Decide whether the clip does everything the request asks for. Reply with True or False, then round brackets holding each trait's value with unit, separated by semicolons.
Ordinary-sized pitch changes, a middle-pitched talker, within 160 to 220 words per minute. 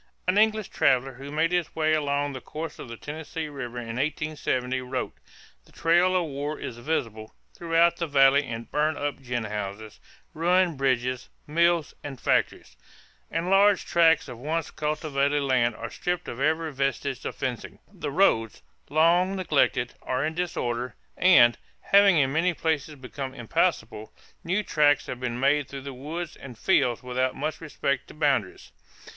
True (4.4 semitones; 145 Hz; 165 wpm)